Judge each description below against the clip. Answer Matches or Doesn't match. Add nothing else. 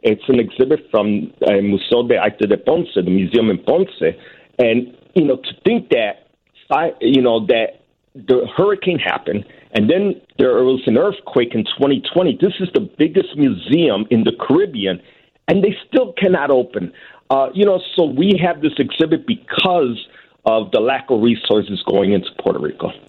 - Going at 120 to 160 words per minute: Doesn't match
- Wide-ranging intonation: Matches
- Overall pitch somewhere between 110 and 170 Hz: Matches